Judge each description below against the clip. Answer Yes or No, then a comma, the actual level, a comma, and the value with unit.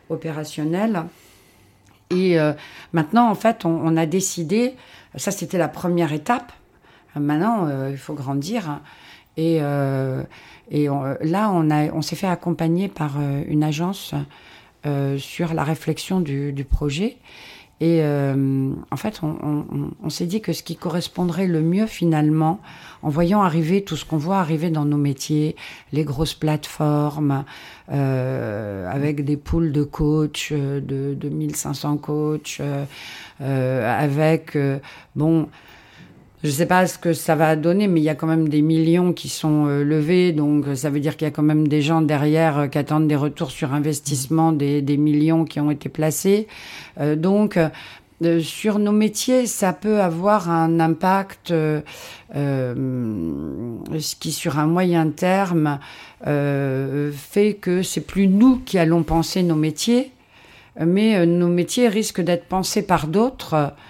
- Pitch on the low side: No, medium, 155 Hz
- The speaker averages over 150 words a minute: Yes, average, 160 wpm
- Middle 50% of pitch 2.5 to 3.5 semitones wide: Yes, average, 3.1 semitones